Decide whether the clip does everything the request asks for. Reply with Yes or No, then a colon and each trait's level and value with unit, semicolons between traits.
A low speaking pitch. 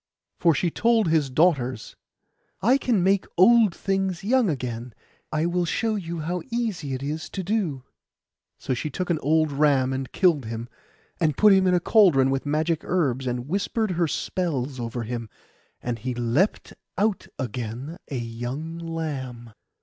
No: medium, 155 Hz